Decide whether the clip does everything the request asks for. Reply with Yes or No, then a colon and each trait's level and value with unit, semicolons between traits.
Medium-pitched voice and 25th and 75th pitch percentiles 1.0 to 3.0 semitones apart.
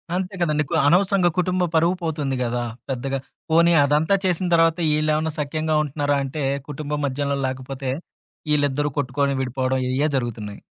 No: medium, 145 Hz; average, 3.4 semitones